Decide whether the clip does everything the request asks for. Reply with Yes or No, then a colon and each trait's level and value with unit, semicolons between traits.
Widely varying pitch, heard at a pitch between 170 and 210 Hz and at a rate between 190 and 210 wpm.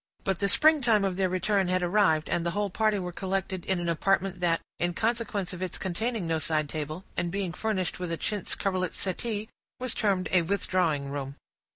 No: average, 2.9 semitones; medium, 185 Hz; average, 200 wpm